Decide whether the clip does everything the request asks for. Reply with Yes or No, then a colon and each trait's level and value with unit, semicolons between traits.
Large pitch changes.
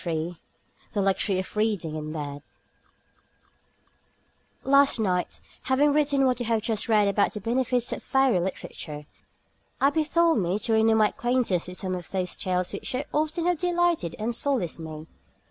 Yes: wide, 6.8 semitones